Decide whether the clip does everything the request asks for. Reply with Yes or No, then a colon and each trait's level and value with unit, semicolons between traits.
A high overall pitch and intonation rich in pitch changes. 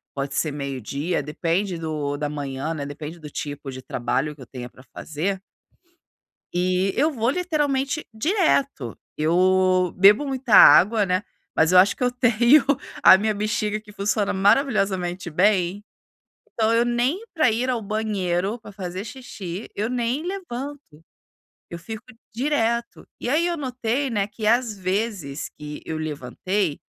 Yes: high, 200 Hz; wide, 6.7 semitones